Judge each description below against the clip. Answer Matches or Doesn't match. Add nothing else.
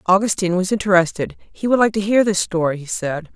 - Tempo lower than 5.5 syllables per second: Doesn't match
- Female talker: Matches